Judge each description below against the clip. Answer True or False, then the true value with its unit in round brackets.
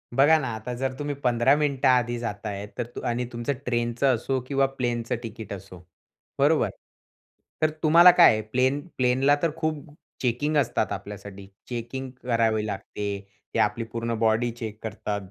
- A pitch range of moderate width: True (3.3 semitones)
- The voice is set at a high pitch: False (120 Hz)